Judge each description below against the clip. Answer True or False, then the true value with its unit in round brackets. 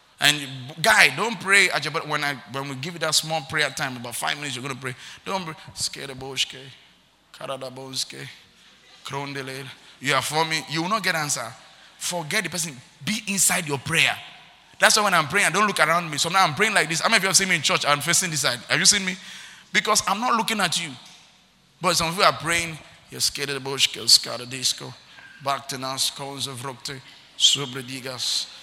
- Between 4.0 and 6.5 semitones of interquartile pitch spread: True (5.1 semitones)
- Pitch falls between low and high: True (155 Hz)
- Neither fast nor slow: False (210 wpm)